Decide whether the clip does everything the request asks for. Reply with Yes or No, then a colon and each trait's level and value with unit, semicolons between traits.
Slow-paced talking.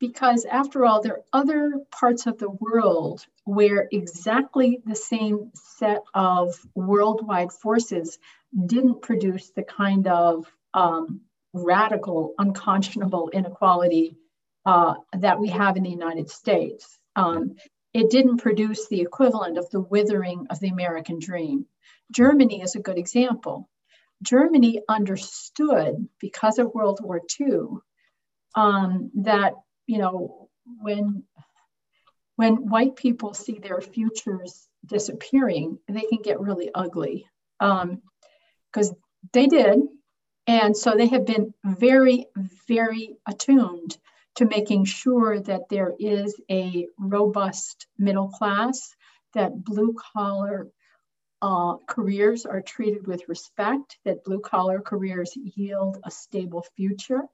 Yes: slow, 120 wpm